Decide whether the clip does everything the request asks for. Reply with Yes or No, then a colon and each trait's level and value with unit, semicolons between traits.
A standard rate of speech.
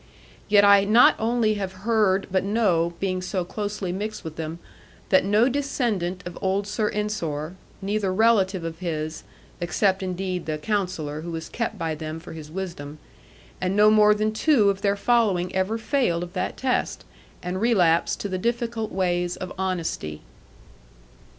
Yes: average, 165 wpm